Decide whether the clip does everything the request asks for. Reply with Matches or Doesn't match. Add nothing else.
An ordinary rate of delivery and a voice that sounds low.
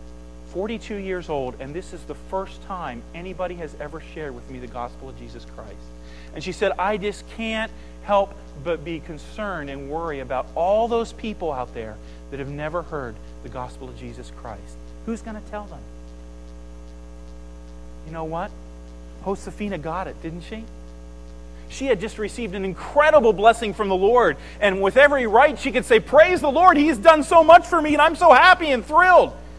Doesn't match